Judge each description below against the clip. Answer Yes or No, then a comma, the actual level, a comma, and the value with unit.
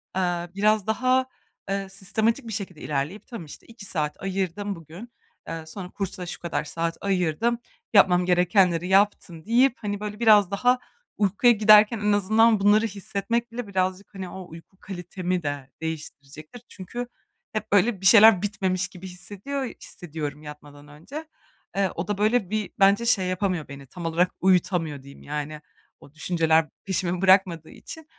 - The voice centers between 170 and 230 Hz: Yes, high, 190 Hz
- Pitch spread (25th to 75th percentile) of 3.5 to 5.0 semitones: Yes, average, 3.9 semitones